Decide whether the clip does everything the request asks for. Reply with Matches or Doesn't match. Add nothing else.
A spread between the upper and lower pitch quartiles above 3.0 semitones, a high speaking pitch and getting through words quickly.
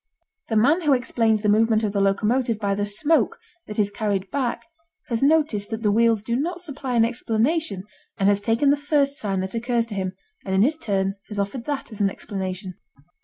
Matches